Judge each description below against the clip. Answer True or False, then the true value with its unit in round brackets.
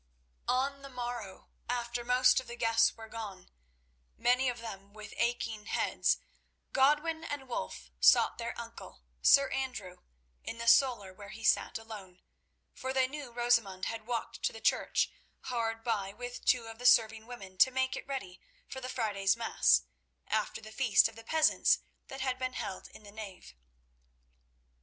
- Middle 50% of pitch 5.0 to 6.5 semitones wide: False (3.4 semitones)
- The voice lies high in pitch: True (235 Hz)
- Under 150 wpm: False (165 wpm)